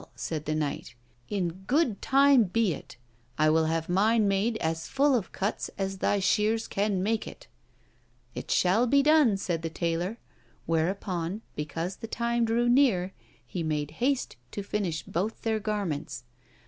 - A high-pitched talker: Yes, high, 195 Hz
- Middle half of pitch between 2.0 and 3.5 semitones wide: No, wide, 5.5 semitones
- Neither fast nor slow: Yes, average, 160 wpm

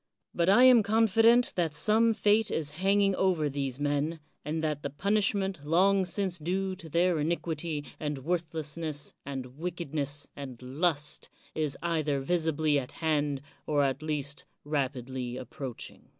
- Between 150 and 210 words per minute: No, average, 140 wpm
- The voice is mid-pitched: Yes, medium, 155 Hz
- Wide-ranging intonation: No, average, 4.3 semitones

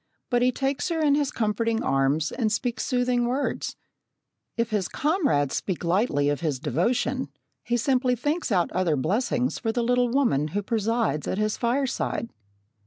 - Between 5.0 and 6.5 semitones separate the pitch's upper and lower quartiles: Yes, wide, 5.6 semitones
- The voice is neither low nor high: No, high, 235 Hz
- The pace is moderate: Yes, average, 165 wpm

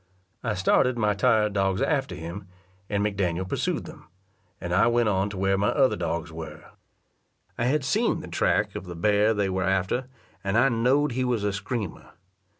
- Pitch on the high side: No, low, 100 Hz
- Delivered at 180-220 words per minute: Yes, average, 185 wpm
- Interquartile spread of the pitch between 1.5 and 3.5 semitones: No, average, 4.3 semitones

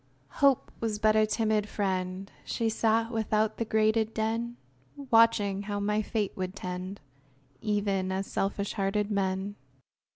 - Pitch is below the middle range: No, high, 210 Hz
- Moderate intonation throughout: No, narrow, 2.1 semitones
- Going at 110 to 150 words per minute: Yes, slow, 135 wpm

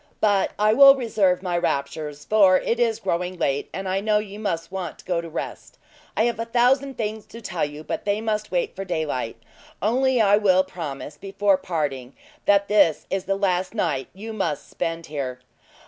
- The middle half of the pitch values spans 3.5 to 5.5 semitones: Yes, average, 4.4 semitones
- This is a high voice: Yes, high, 195 Hz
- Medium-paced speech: Yes, average, 195 wpm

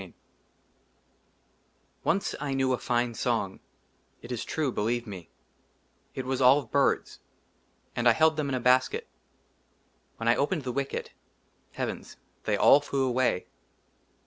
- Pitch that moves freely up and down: No, narrow, 2.6 semitones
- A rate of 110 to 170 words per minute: Yes, average, 145 wpm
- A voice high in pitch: No, low, 130 Hz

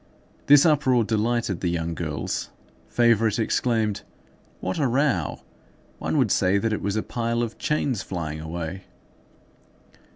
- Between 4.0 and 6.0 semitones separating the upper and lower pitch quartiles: Yes, average, 4.7 semitones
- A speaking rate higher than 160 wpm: No, slow, 135 wpm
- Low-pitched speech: Yes, low, 110 Hz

